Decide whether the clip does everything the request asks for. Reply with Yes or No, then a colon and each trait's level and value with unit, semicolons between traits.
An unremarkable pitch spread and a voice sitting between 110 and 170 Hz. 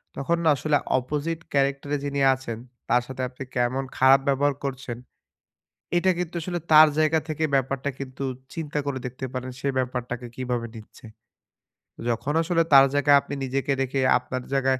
No: narrow, 2.3 semitones; low, 135 Hz